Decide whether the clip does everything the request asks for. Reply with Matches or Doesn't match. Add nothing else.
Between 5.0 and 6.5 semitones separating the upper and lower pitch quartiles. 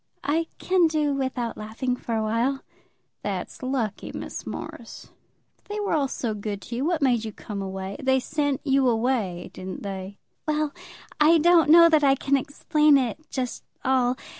Matches